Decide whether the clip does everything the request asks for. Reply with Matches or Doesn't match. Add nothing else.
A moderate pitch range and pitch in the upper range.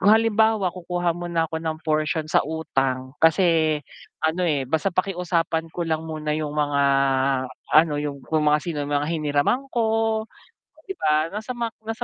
Doesn't match